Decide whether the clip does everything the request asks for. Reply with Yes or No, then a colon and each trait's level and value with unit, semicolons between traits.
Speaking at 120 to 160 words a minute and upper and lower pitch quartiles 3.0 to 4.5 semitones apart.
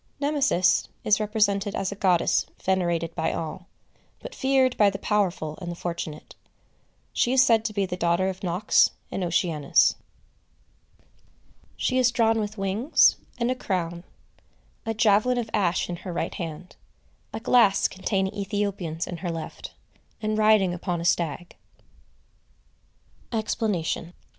Yes: average, 140 wpm; average, 4.0 semitones